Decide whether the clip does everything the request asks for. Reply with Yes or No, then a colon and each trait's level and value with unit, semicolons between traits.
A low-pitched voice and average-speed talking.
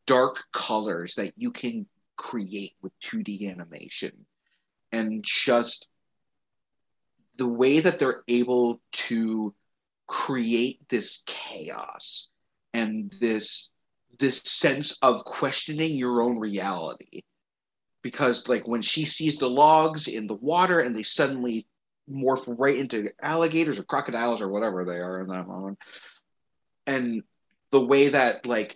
No: low, 120 Hz; slow, 125 wpm